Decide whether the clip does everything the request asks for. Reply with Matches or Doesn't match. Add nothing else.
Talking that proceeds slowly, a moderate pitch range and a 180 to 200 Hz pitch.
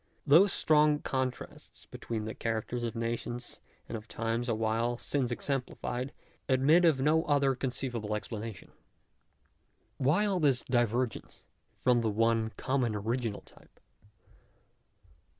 Doesn't match